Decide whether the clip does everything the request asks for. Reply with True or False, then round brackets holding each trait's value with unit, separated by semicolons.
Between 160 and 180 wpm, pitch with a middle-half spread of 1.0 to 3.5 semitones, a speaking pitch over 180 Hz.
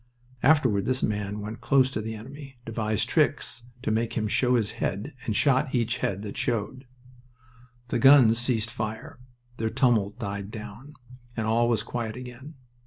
False (165 wpm; 3.0 semitones; 115 Hz)